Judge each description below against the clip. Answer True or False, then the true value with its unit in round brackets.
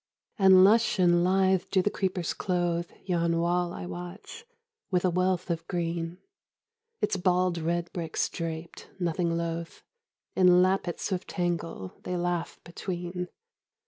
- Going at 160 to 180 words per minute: False (135 wpm)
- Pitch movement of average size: False (1.4 semitones)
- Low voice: False (175 Hz)